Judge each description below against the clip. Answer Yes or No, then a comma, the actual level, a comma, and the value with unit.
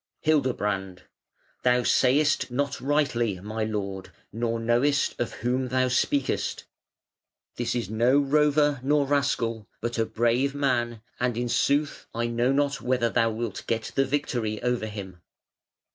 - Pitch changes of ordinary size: Yes, average, 3.4 semitones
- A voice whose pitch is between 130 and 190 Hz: No, low, 120 Hz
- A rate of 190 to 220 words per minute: No, average, 140 wpm